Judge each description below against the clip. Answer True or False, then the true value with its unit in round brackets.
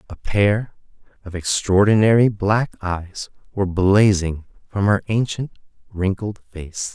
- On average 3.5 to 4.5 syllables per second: True (4.0 syllables/s)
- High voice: False (100 Hz)